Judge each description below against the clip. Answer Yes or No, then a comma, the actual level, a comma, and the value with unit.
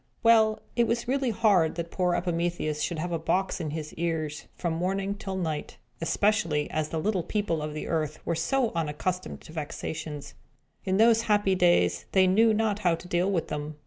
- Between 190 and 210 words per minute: Yes, average, 195 wpm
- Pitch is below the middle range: No, medium, 175 Hz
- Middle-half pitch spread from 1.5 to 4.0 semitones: No, average, 4.5 semitones